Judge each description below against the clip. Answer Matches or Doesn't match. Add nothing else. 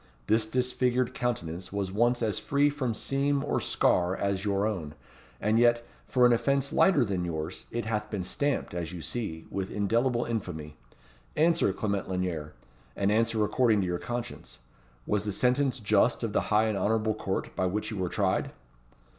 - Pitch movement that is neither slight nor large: Matches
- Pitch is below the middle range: Matches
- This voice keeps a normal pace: Matches